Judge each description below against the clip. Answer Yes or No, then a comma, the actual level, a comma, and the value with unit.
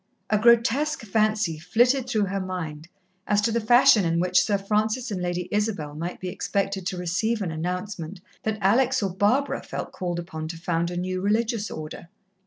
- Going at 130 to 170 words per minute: No, average, 185 wpm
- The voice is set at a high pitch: Yes, high, 195 Hz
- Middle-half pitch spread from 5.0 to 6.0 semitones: No, average, 3.8 semitones